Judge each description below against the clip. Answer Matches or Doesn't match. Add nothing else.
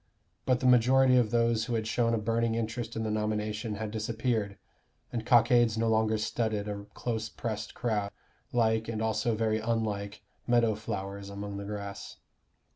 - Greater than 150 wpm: Matches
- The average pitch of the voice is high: Doesn't match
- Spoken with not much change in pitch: Matches